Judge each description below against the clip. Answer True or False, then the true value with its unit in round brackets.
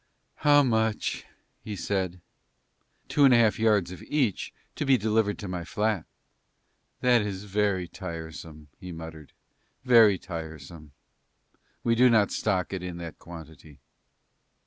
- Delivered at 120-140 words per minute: True (135 wpm)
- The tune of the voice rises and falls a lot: False (4.8 semitones)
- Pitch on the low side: True (95 Hz)